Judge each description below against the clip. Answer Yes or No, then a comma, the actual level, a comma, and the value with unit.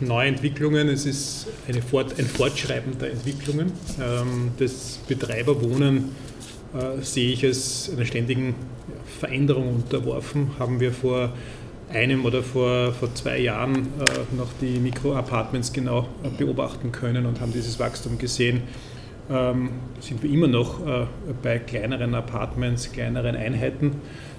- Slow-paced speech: Yes, slow, 115 wpm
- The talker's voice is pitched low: Yes, low, 125 Hz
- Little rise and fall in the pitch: Yes, narrow, 1.9 semitones